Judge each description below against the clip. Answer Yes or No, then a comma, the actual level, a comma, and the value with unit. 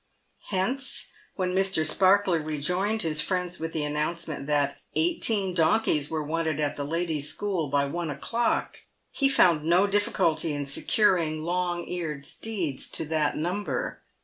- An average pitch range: Yes, average, 4.0 semitones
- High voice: No, medium, 165 Hz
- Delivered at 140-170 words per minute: Yes, average, 145 wpm